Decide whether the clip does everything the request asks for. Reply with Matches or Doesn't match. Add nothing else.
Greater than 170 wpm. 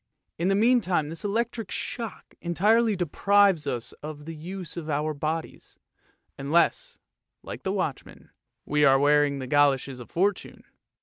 Doesn't match